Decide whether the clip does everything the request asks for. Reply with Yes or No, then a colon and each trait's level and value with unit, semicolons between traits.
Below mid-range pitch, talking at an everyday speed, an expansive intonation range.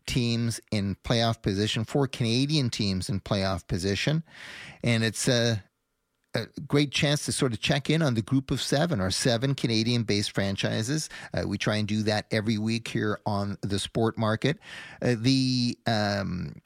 No: low, 115 Hz; average, 170 wpm; average, 4.1 semitones